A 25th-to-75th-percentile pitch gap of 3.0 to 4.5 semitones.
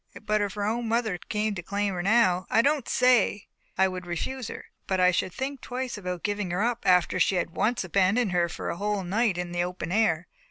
Yes: average, 3.9 semitones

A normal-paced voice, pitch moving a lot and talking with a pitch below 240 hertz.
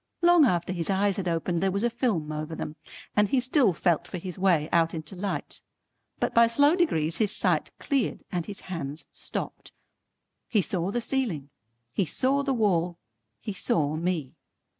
Yes: average, 180 wpm; wide, 5.9 semitones; medium, 185 Hz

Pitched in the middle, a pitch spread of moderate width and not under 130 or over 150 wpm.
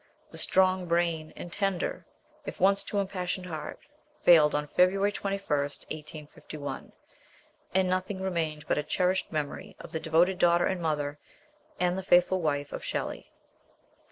Yes: medium, 175 Hz; average, 3.5 semitones; average, 145 wpm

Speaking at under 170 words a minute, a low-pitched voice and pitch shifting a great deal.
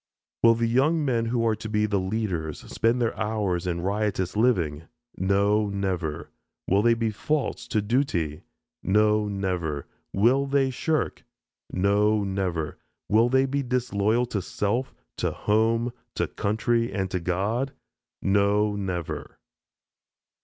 No: slow, 135 wpm; low, 105 Hz; average, 3.5 semitones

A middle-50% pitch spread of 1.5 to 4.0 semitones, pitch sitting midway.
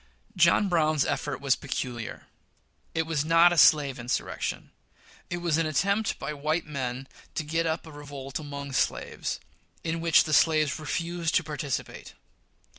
Yes: average, 2.8 semitones; medium, 155 Hz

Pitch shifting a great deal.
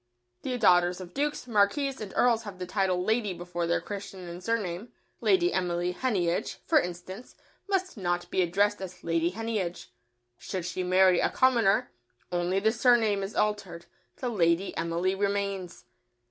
No: average, 3.7 semitones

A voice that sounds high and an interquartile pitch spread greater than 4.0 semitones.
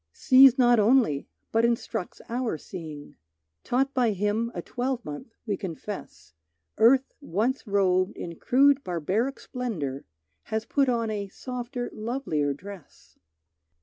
Yes: high, 225 Hz; wide, 5.4 semitones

